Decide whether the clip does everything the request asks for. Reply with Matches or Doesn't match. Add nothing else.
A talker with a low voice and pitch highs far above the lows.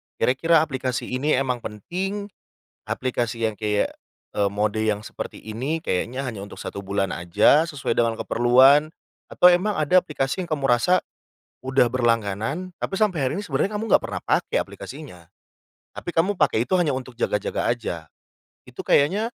Matches